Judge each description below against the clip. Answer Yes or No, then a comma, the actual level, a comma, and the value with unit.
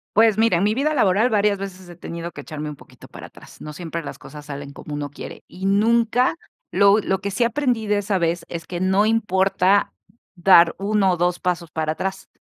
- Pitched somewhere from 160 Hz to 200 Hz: Yes, high, 190 Hz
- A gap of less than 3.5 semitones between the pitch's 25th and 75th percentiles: No, average, 3.8 semitones